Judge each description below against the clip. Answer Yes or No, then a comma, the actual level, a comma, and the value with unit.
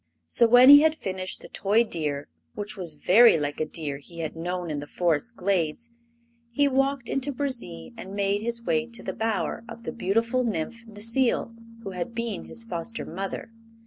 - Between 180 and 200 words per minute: Yes, average, 185 wpm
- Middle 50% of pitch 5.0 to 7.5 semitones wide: Yes, wide, 5.5 semitones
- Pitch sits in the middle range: No, high, 215 Hz